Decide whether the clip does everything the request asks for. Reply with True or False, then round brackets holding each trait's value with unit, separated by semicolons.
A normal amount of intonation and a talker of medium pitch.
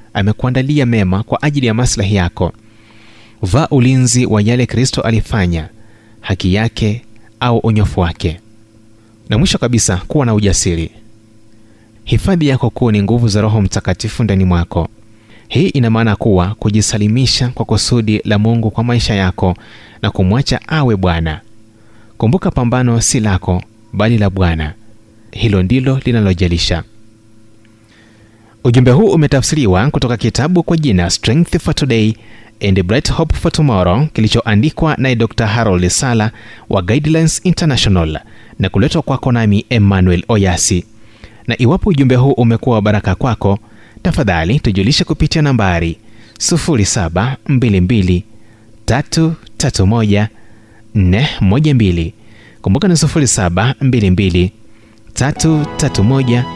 False (3.4 semitones; 110 Hz)